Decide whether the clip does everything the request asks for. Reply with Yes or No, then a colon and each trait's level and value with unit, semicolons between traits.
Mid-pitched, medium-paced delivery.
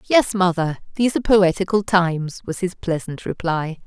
Yes: medium, 180 Hz; average, 155 wpm